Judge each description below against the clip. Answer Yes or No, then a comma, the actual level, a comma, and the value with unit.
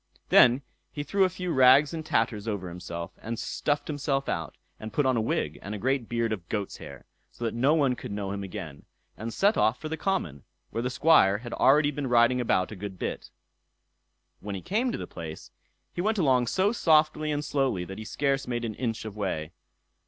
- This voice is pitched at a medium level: No, low, 120 Hz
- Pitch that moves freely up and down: Yes, wide, 6.3 semitones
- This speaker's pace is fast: Yes, fast, 210 wpm